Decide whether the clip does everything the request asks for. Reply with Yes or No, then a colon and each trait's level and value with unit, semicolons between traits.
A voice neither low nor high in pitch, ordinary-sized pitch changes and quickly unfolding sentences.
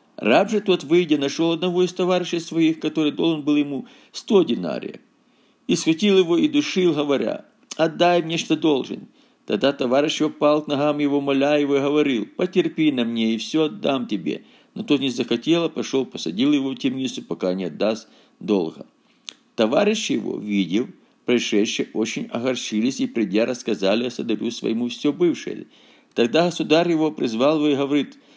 Yes: medium, 150 Hz; average, 4.7 semitones; fast, 165 wpm